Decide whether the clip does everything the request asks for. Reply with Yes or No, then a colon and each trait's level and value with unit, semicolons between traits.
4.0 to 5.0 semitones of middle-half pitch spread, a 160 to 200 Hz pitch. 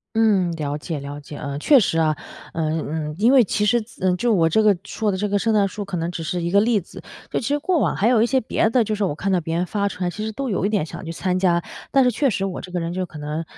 Yes: average, 4.7 semitones; high, 195 Hz